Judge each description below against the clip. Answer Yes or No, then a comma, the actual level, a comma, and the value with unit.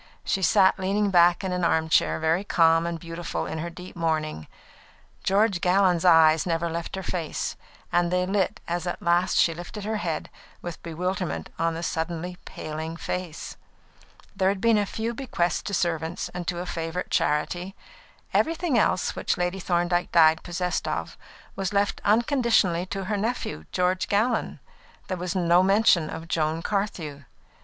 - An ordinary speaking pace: Yes, average, 165 wpm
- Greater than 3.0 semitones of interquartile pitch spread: No, narrow, 2.6 semitones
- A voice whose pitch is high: No, medium, 175 Hz